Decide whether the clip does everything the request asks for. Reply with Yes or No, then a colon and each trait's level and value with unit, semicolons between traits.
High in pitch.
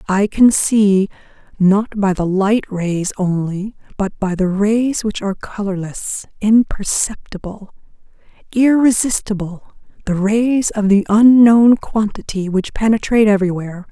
Yes: high, 205 Hz